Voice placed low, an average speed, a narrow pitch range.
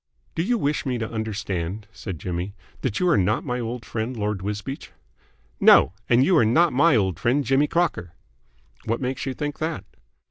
No: low, 120 Hz; average, 180 wpm; wide, 5.5 semitones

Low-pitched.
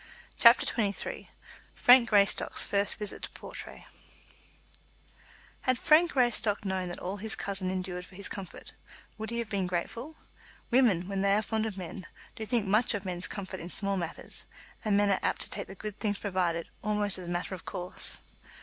No: high, 200 Hz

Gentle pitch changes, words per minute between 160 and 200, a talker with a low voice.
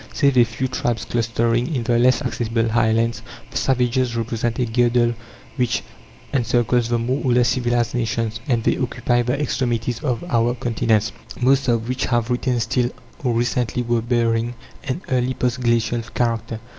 Yes: narrow, 1.3 semitones; average, 165 wpm; low, 120 Hz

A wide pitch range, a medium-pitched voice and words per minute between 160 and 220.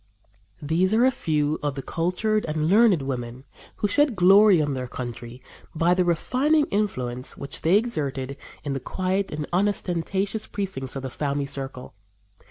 Yes: wide, 6.7 semitones; medium, 160 Hz; average, 165 wpm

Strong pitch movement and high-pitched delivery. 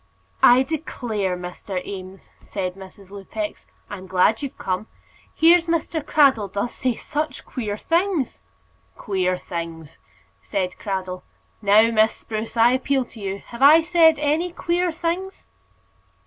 Yes: wide, 8.3 semitones; high, 225 Hz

